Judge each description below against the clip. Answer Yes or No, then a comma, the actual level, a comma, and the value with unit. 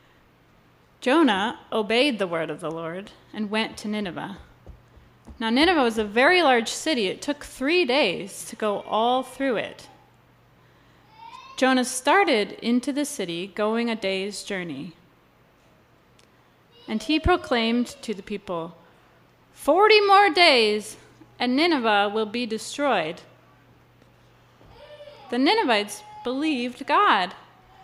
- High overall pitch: Yes, high, 245 Hz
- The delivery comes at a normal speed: No, slow, 115 wpm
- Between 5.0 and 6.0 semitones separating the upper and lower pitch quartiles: Yes, average, 5.3 semitones